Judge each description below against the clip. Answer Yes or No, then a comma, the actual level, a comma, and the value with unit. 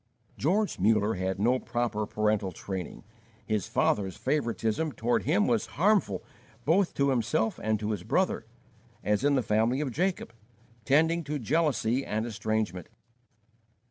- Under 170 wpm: Yes, average, 140 wpm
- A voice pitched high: No, low, 115 Hz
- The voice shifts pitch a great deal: Yes, wide, 5.8 semitones